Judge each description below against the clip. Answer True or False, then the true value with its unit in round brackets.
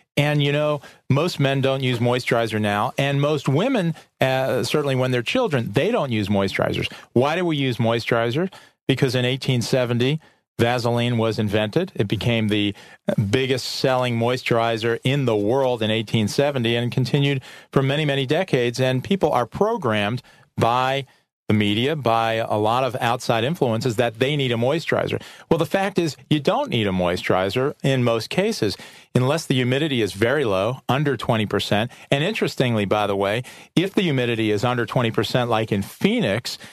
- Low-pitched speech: True (125 Hz)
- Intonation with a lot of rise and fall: False (3.7 semitones)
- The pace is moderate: True (165 wpm)